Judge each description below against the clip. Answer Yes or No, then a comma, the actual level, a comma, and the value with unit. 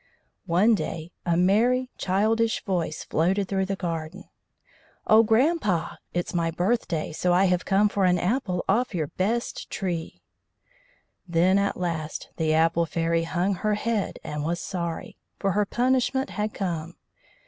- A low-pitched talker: No, medium, 185 Hz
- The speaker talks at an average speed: Yes, average, 150 wpm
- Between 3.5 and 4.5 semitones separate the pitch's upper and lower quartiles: Yes, average, 4.0 semitones